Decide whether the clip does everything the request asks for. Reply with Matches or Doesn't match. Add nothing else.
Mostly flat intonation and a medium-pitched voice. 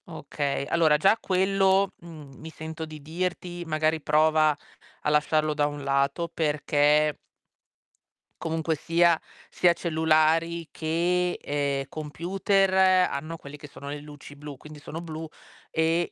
Matches